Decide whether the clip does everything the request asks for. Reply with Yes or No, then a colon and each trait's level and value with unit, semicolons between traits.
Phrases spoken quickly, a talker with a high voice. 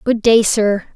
No: average, 190 wpm; high, 215 Hz